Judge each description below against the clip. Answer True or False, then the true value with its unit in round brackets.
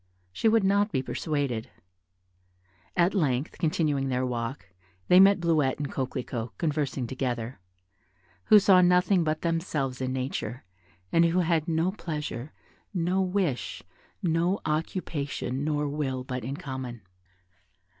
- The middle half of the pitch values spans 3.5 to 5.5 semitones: True (5.1 semitones)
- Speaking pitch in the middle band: True (150 Hz)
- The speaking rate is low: True (125 wpm)